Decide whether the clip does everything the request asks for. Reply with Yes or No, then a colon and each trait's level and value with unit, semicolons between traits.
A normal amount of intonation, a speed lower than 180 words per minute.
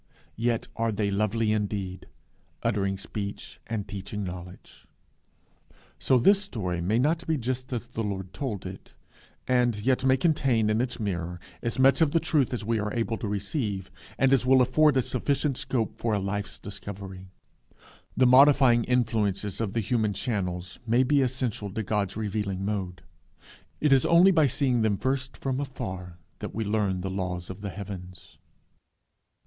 Yes: average, 4.6 semitones; average, 165 wpm